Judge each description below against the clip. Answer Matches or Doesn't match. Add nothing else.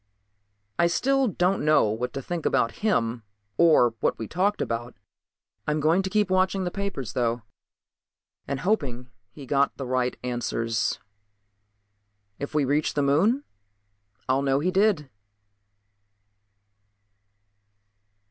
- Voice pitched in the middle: Matches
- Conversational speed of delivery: Doesn't match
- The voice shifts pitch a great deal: Matches